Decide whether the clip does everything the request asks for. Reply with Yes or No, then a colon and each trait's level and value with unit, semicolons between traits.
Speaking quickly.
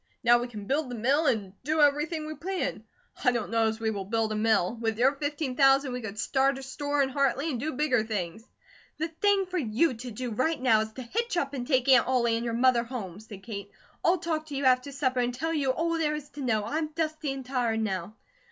Yes: fast, 245 wpm